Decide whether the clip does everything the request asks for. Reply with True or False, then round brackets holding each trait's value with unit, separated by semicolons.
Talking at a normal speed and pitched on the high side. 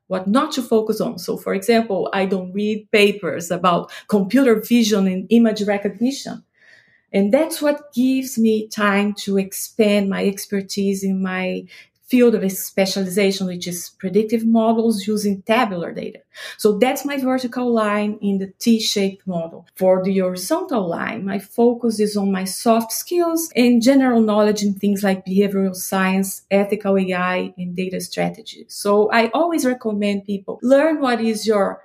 True (155 wpm; 210 Hz)